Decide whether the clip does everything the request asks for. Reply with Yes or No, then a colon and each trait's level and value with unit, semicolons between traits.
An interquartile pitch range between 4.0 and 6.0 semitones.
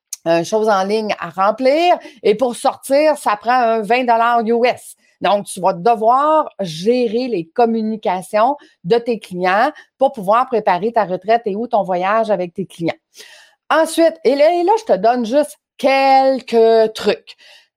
Yes: average, 4.6 semitones